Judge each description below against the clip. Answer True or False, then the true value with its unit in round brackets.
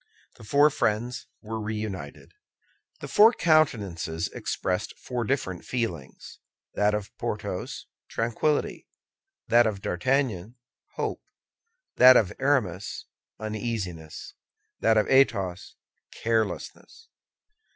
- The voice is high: False (110 Hz)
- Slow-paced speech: True (95 wpm)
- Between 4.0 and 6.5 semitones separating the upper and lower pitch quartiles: True (5.0 semitones)